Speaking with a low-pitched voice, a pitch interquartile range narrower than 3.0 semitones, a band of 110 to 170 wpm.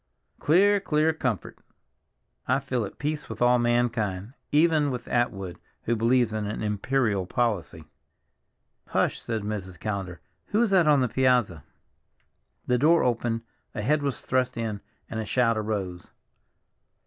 No: low, 120 Hz; average, 4.5 semitones; average, 140 wpm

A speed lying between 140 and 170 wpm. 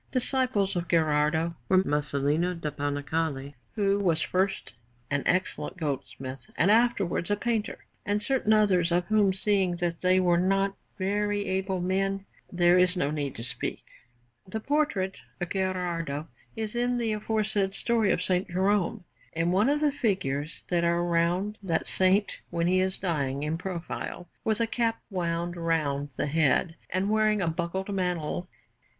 Yes: average, 155 wpm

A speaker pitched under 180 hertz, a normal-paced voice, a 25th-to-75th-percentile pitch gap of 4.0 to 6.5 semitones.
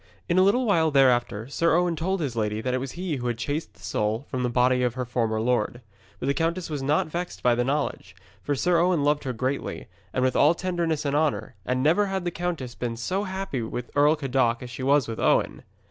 No: low, 135 Hz; fast, 240 wpm; wide, 5.4 semitones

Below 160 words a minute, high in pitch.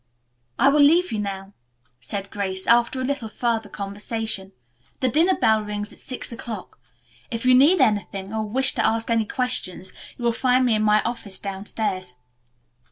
No: average, 170 wpm; high, 220 Hz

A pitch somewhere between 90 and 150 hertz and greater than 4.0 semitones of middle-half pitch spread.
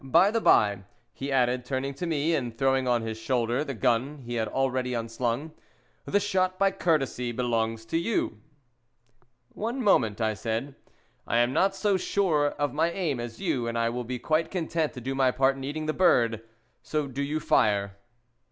Yes: low, 135 Hz; average, 5.1 semitones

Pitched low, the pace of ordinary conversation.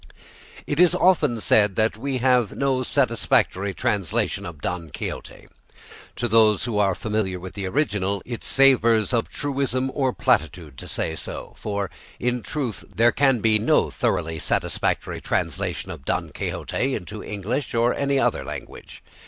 Yes: low, 115 Hz; average, 150 wpm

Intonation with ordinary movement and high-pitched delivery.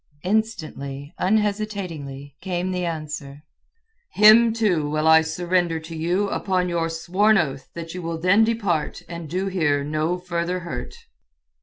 No: average, 3.9 semitones; medium, 175 Hz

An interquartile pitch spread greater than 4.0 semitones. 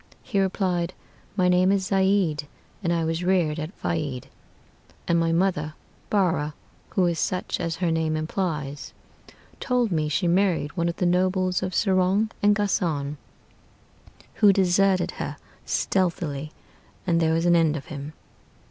No: average, 3.0 semitones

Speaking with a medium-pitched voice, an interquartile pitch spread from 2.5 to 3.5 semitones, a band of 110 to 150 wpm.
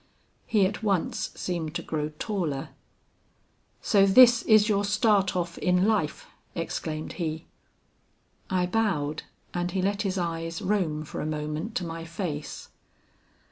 No: medium, 180 Hz; average, 4.1 semitones; average, 140 wpm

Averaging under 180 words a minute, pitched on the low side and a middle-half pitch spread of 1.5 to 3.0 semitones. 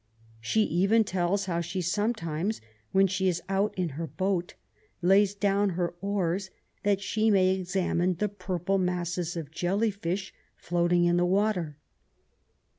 No: average, 145 wpm; medium, 185 Hz; narrow, 2.4 semitones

